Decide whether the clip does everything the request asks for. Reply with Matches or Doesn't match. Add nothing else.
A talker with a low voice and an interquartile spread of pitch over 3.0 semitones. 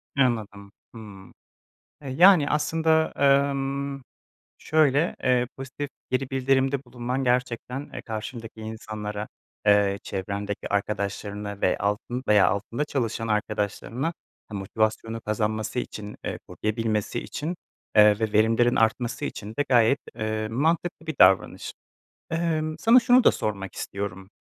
Matches